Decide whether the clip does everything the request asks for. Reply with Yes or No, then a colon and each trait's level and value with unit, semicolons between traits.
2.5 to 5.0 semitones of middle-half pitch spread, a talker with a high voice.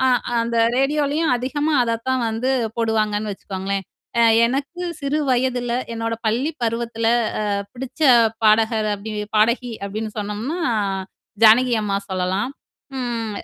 Yes: average, 3.4 semitones; high, 230 Hz